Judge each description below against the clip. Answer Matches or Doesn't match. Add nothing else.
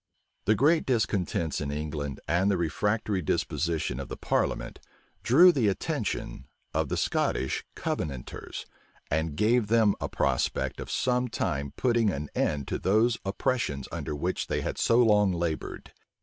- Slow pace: Doesn't match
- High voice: Doesn't match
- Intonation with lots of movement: Matches